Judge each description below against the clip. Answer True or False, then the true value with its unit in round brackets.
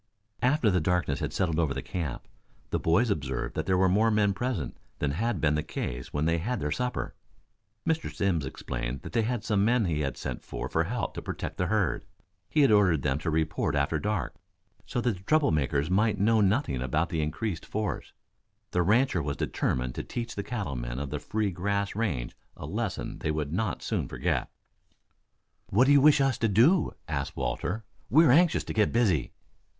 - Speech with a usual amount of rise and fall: False (6.8 semitones)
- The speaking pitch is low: True (95 Hz)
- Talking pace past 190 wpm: True (200 wpm)